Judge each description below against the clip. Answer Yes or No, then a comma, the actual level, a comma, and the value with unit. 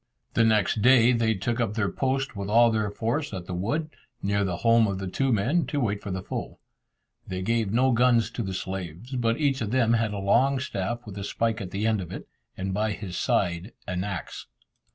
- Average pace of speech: No, fast, 225 wpm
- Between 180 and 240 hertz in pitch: No, low, 110 Hz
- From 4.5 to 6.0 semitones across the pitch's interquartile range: No, average, 3.5 semitones